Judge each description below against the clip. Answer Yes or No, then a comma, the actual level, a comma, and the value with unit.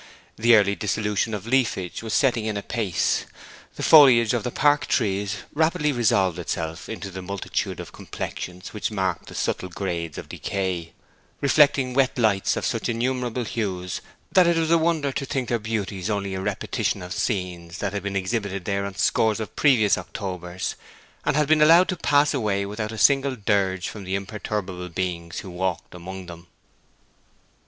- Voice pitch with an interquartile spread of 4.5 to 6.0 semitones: Yes, average, 4.9 semitones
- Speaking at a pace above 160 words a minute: Yes, average, 175 wpm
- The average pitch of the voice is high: No, low, 105 Hz